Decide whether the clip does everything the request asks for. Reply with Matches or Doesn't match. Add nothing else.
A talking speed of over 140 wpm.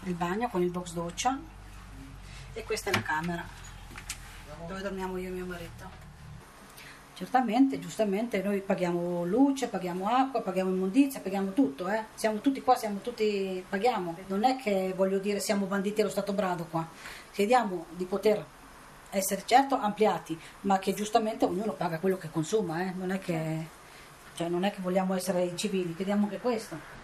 Matches